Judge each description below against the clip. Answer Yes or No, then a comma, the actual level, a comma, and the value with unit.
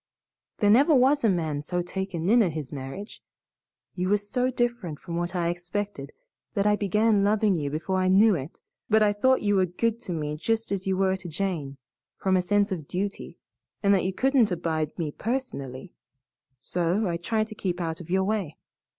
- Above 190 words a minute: Yes, average, 200 wpm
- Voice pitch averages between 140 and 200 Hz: Yes, high, 190 Hz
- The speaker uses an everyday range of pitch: Yes, average, 3.8 semitones